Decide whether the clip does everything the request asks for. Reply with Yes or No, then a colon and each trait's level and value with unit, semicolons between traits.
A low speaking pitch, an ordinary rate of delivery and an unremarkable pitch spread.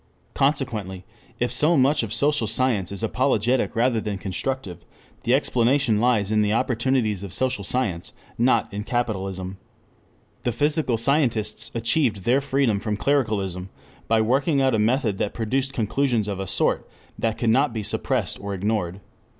Yes: low, 115 Hz; average, 155 wpm; average, 4.2 semitones